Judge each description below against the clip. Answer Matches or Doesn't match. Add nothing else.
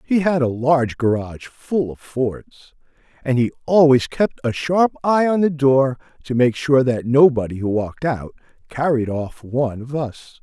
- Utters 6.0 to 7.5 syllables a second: Doesn't match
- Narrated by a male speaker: Matches